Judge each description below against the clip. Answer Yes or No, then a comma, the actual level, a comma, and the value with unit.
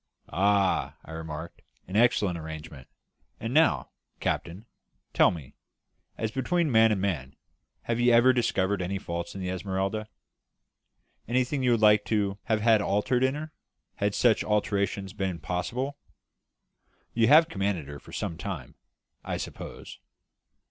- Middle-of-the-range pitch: No, low, 100 Hz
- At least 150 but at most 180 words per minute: No, average, 140 wpm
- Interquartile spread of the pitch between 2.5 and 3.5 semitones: No, average, 4.7 semitones